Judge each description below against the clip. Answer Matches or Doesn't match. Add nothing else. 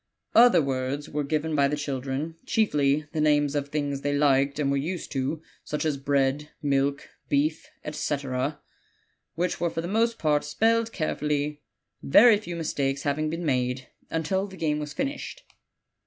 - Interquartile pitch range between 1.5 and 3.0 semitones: Matches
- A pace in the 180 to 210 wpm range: Doesn't match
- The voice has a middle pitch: Matches